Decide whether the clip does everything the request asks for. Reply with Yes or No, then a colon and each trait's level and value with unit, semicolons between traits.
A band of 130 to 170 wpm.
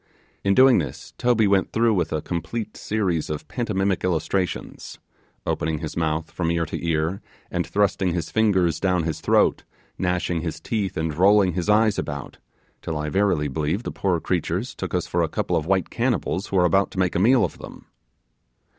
No: average, 190 wpm